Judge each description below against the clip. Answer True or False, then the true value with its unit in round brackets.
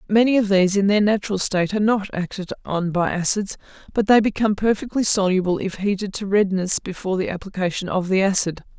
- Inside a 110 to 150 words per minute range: False (190 wpm)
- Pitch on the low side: False (195 Hz)